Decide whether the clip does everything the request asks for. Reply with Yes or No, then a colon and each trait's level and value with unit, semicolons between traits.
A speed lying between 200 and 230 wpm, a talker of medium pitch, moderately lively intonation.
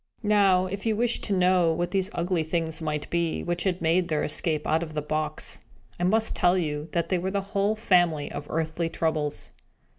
Yes: fast, 205 wpm; medium, 175 Hz; average, 3.0 semitones